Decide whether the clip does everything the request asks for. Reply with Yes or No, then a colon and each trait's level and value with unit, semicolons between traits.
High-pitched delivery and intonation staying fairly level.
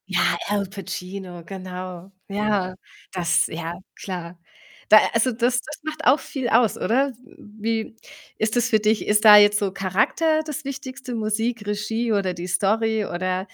No: high, 210 Hz; average, 3.6 semitones